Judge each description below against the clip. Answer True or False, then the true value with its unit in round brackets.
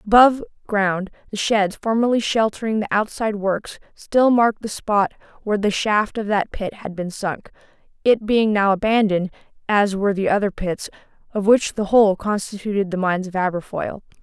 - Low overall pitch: False (205 Hz)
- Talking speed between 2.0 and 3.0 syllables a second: False (5.4 syllables/s)